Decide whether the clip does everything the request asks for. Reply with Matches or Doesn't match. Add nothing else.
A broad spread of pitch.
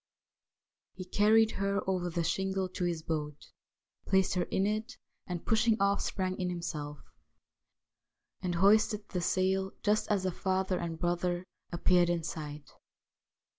Doesn't match